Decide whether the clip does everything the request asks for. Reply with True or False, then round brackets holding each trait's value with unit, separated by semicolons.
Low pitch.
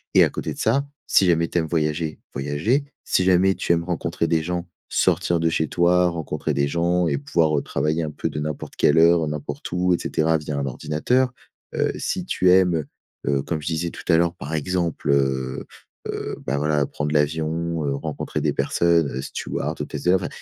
True (80 Hz)